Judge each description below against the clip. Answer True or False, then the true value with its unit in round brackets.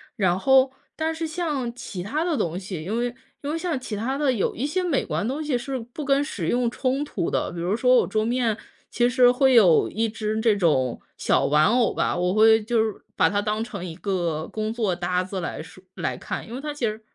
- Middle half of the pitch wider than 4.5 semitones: True (5.6 semitones)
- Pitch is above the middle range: True (225 Hz)